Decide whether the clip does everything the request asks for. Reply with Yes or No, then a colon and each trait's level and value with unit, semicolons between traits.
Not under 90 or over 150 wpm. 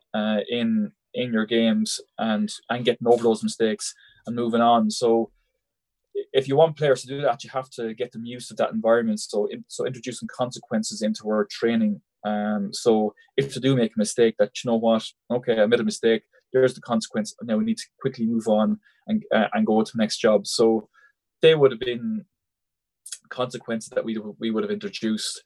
No: fast, 205 wpm